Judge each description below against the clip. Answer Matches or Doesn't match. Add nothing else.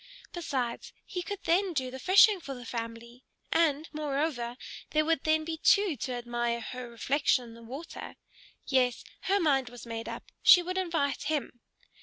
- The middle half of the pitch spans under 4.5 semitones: Doesn't match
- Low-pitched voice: Doesn't match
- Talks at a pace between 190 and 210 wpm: Doesn't match